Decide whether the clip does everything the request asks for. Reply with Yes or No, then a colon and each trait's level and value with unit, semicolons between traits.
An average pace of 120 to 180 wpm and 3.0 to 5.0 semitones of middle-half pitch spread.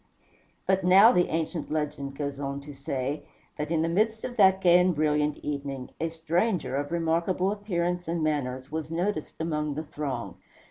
Yes: average, 175 wpm; average, 3.5 semitones